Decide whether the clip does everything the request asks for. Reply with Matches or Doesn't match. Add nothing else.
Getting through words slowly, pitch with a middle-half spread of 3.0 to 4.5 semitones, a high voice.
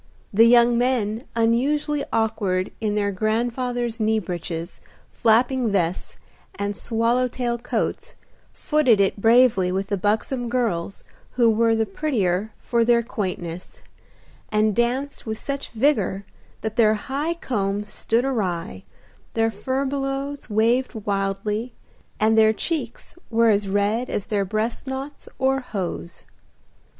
Matches